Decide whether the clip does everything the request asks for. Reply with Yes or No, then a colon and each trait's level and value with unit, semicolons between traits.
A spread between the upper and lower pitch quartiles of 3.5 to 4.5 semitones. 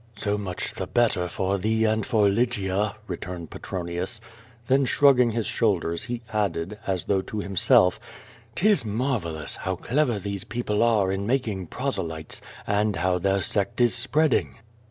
Yes: average, 4.1 semitones